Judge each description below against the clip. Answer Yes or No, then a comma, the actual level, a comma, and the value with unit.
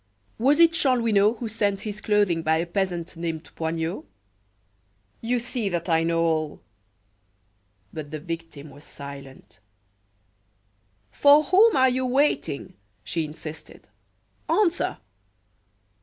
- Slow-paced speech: Yes, slow, 120 wpm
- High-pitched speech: No, medium, 170 Hz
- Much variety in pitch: Yes, wide, 7.2 semitones